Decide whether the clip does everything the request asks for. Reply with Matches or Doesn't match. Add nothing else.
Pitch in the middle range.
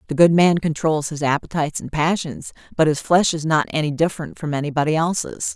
Matches